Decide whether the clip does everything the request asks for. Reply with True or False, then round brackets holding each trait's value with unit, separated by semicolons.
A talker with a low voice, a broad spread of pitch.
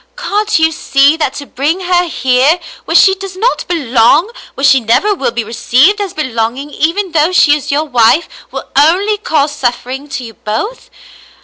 False (295 Hz; 5.9 semitones)